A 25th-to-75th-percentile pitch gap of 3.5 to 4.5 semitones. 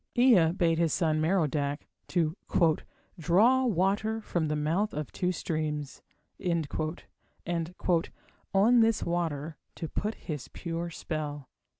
Yes: average, 3.8 semitones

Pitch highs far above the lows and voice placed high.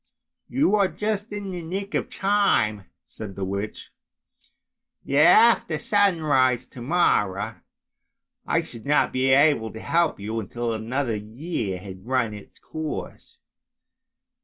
No: wide, 8.3 semitones; low, 130 Hz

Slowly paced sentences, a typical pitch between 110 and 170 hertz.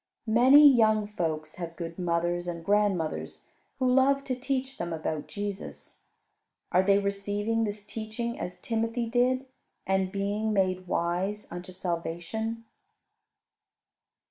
No: slow, 120 wpm; high, 205 Hz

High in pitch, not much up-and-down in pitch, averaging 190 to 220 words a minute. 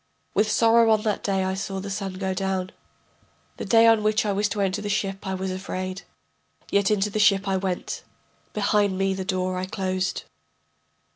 Yes: high, 195 Hz; narrow, 1.8 semitones; average, 195 wpm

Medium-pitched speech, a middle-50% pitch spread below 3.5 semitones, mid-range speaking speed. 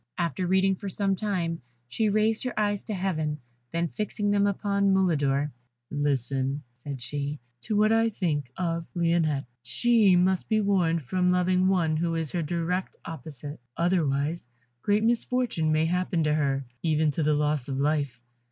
No: medium, 170 Hz; average, 4.7 semitones; average, 160 wpm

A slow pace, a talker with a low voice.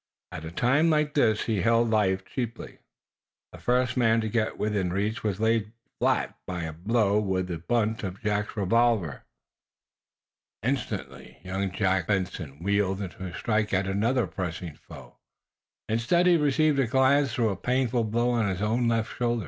No: average, 155 wpm; low, 110 Hz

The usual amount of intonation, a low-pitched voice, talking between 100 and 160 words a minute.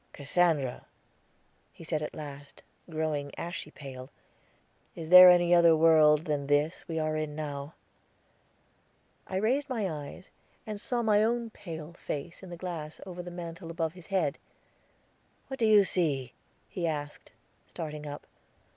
No: average, 3.4 semitones; medium, 165 Hz; average, 145 wpm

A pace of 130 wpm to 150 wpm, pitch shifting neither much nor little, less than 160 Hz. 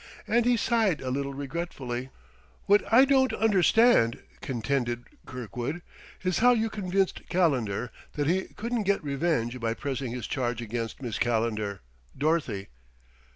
No: slow, 135 wpm; wide, 8.4 semitones; medium, 140 Hz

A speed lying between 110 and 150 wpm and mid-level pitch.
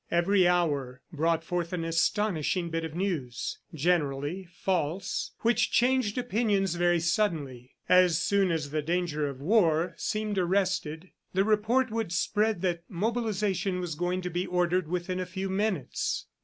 Yes: average, 145 wpm; medium, 180 Hz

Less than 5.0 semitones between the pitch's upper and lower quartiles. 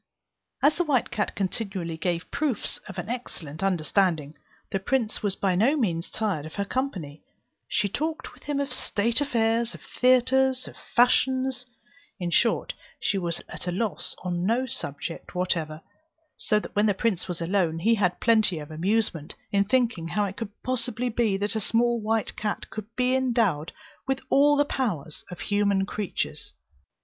No: wide, 5.4 semitones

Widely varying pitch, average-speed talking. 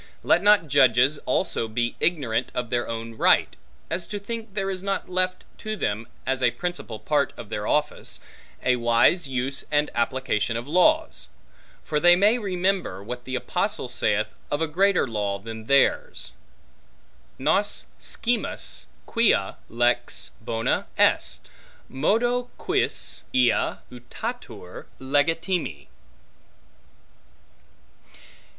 No: wide, 7.6 semitones; slow, 120 wpm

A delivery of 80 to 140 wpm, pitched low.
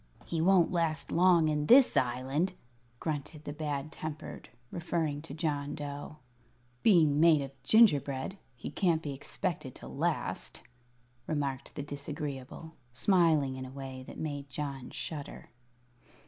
No: slow, 135 wpm; medium, 150 Hz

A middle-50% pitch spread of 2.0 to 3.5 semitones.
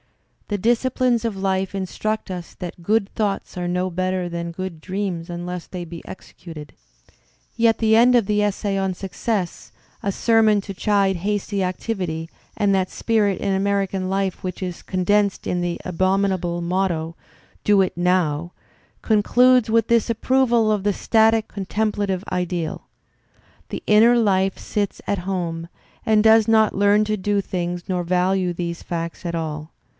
Yes: average, 3.0 semitones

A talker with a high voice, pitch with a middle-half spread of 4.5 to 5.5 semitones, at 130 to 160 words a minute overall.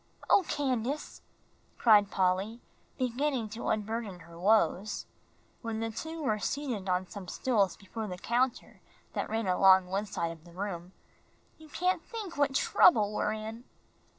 Yes: high, 215 Hz; average, 4.9 semitones; average, 150 wpm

